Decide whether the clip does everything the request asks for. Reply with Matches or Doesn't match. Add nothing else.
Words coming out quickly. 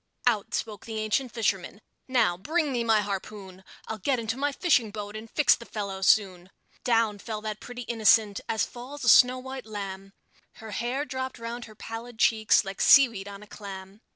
Doesn't match